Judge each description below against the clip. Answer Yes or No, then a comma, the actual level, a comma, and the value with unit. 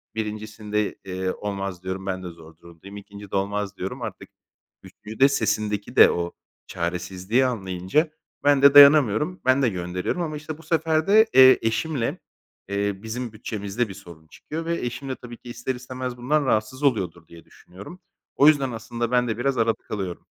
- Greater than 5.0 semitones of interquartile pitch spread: Yes, wide, 5.4 semitones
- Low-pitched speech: Yes, low, 110 Hz